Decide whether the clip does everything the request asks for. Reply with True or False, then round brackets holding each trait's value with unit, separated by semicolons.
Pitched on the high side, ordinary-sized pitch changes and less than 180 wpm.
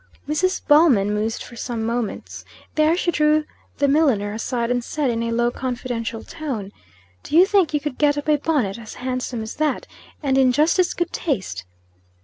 False (260 Hz; 4.9 semitones; 185 wpm)